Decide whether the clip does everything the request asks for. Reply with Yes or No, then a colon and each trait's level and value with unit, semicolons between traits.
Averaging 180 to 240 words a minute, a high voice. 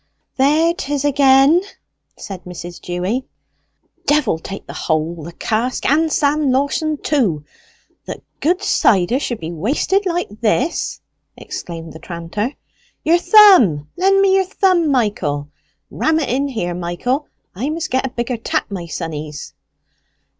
No: average, 140 wpm; very high, 255 Hz